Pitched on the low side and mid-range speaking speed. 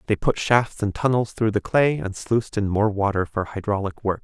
No: low, 105 Hz; fast, 225 wpm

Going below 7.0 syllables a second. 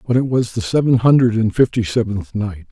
Yes: 5.5 syllables/s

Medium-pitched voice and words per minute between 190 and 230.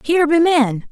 No: very high, 295 Hz; average, 195 wpm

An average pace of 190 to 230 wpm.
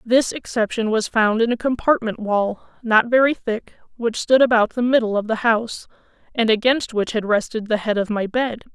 Yes: average, 200 wpm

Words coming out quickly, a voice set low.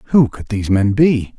Yes: fast, 215 wpm; low, 115 Hz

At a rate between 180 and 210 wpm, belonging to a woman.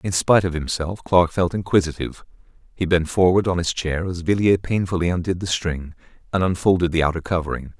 No: average, 185 wpm; male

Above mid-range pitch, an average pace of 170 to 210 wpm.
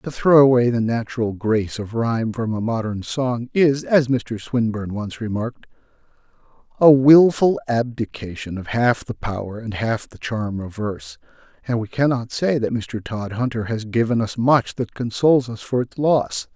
No: low, 115 Hz; average, 175 wpm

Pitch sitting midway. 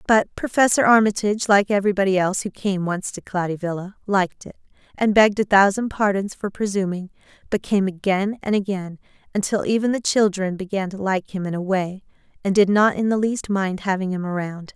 No: high, 195 Hz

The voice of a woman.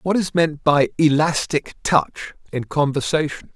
No: male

